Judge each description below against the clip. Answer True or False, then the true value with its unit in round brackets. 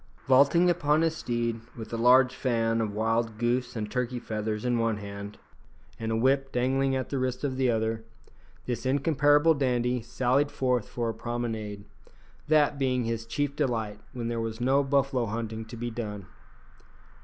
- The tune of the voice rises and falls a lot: False (3.0 semitones)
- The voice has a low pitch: True (120 Hz)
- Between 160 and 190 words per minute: True (170 wpm)